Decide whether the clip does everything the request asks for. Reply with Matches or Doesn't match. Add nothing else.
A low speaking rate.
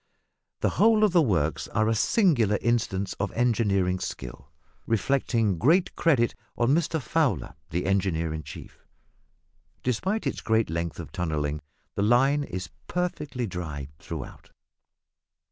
Matches